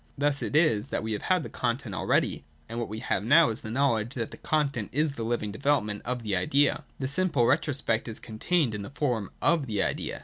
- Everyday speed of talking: No, fast, 235 wpm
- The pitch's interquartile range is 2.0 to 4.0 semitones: No, average, 4.6 semitones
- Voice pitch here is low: Yes, low, 120 Hz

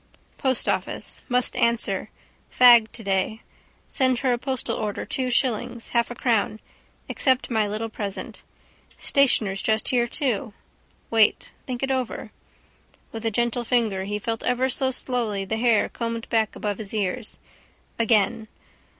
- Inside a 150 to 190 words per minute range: No, average, 140 wpm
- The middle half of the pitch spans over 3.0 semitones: No, narrow, 2.6 semitones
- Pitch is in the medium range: No, high, 230 Hz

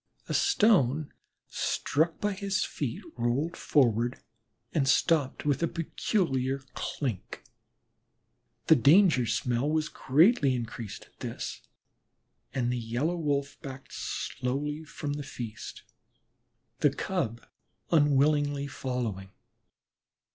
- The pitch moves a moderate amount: Yes, average, 4.1 semitones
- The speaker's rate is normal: No, slow, 105 wpm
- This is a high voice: No, medium, 140 Hz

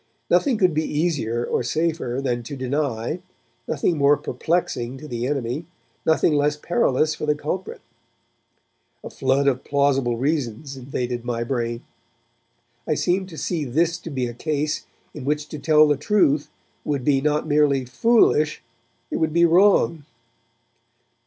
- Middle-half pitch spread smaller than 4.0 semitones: Yes, average, 3.6 semitones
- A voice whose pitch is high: No, medium, 145 Hz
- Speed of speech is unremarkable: Yes, average, 150 wpm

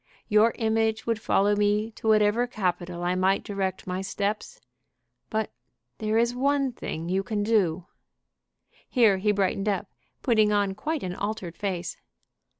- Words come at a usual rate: Yes, average, 150 wpm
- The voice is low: No, high, 210 Hz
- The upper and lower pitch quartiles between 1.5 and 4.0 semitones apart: Yes, narrow, 2.6 semitones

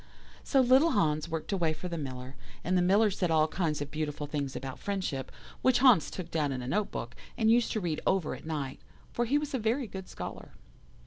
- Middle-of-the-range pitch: Yes, medium, 170 Hz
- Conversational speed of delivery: No, fast, 220 wpm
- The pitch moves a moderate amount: No, wide, 6.6 semitones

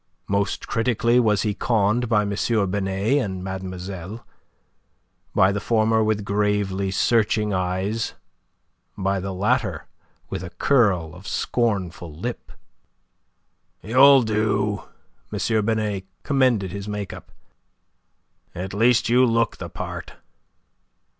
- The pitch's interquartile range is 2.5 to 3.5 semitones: Yes, average, 3.0 semitones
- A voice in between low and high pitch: No, low, 105 Hz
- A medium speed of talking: No, slow, 115 wpm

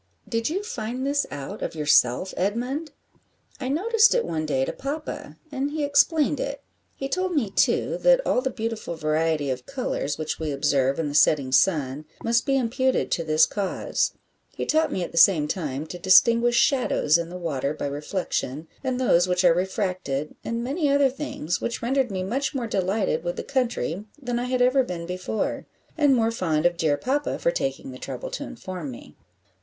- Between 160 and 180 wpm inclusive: No, average, 190 wpm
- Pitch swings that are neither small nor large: No, wide, 9.0 semitones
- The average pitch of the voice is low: No, high, 195 Hz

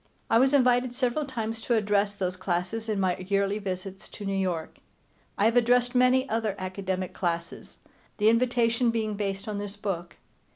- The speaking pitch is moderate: No, high, 210 Hz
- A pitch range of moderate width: Yes, average, 3.8 semitones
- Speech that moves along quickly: No, average, 170 wpm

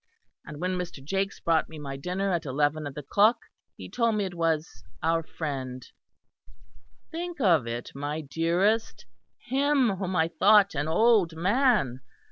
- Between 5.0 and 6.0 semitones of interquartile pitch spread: Yes, wide, 5.6 semitones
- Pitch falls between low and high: Yes, medium, 170 Hz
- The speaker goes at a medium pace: Yes, average, 155 wpm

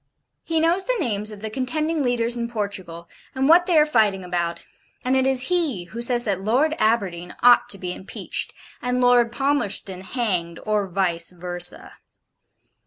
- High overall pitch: Yes, high, 230 Hz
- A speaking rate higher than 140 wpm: Yes, average, 170 wpm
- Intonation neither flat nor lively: No, wide, 5.9 semitones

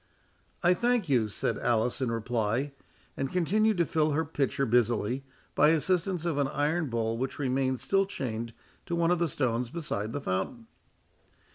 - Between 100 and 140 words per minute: No, average, 165 wpm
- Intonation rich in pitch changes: Yes, wide, 6.1 semitones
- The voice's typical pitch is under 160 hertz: Yes, medium, 140 Hz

